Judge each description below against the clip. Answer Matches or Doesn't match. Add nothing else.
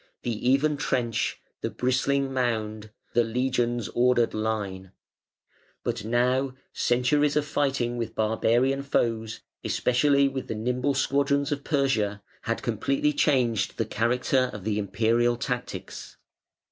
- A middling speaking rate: Doesn't match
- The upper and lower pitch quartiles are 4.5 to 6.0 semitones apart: Doesn't match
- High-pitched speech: Doesn't match